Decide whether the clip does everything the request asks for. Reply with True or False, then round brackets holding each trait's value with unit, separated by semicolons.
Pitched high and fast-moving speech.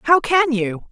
False (270 Hz; 195 wpm)